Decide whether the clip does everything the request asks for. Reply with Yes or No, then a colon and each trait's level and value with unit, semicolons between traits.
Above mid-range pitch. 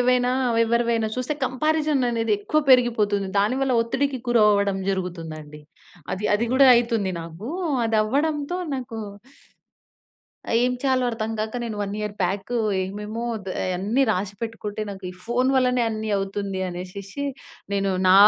Yes: high, 220 Hz